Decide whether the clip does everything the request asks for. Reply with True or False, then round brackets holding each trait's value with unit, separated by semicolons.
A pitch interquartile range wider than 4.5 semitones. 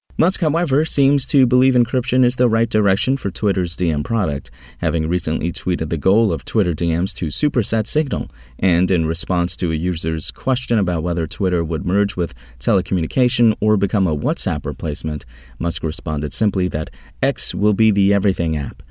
True (5.6 semitones)